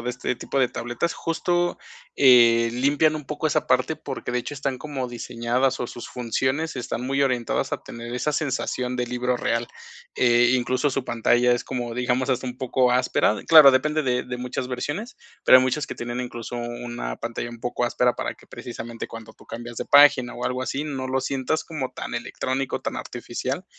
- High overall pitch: No, low, 125 Hz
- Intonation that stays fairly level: Yes, narrow, 2.1 semitones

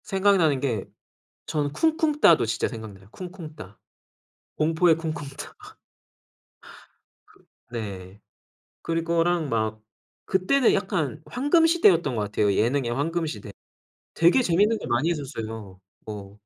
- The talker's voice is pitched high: No, medium, 155 Hz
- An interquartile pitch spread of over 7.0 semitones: Yes, wide, 8.2 semitones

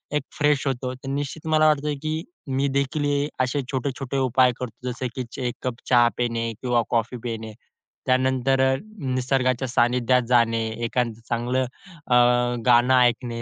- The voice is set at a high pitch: No, low, 130 Hz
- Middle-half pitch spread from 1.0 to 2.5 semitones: Yes, narrow, 2.2 semitones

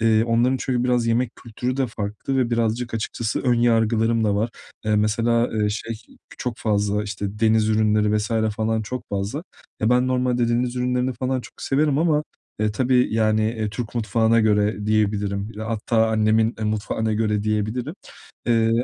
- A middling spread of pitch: No, narrow, 2.3 semitones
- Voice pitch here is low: Yes, low, 110 Hz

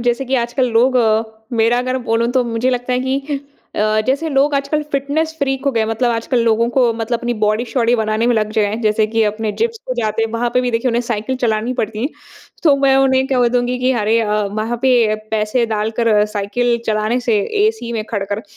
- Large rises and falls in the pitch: No, average, 2.9 semitones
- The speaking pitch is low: No, high, 235 Hz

